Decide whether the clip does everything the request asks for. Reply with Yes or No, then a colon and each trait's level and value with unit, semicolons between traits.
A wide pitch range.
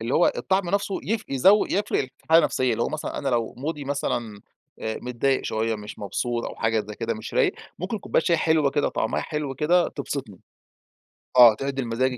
Yes: wide, 5.7 semitones